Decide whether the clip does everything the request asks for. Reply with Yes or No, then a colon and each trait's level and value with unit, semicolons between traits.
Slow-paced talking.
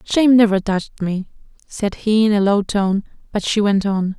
No: average, 200 wpm